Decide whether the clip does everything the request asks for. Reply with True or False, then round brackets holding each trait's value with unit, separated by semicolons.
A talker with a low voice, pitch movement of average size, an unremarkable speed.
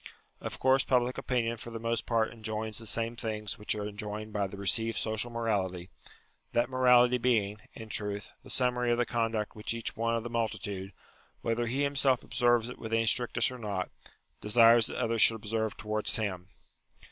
False (115 Hz; 2.1 semitones; 190 wpm)